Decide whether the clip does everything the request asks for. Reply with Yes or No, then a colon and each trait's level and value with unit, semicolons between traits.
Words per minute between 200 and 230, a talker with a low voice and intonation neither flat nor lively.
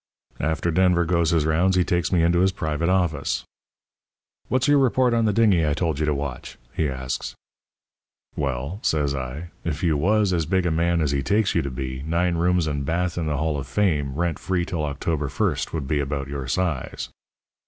Yes: fast, 205 wpm; very low, 80 Hz; average, 3.8 semitones